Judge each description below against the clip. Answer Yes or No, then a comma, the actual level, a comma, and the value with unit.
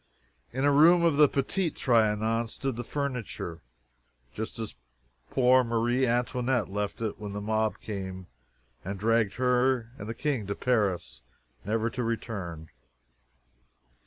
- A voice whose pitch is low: Yes, low, 115 Hz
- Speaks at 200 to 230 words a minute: No, slow, 135 wpm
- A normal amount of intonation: Yes, average, 3.8 semitones